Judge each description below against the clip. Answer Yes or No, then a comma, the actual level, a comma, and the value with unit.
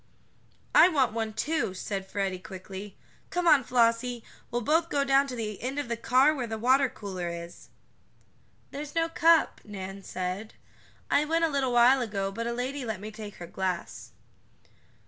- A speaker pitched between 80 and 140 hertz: No, high, 235 Hz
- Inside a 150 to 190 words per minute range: Yes, average, 175 wpm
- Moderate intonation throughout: No, wide, 5.8 semitones